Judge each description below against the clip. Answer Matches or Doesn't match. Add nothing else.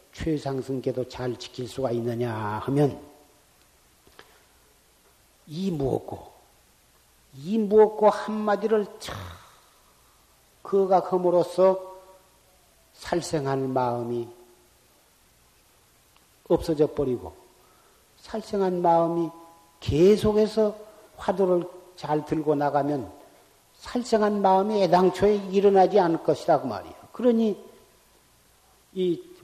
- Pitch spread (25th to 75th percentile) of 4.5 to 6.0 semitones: Doesn't match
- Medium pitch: Matches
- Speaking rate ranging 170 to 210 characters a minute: Matches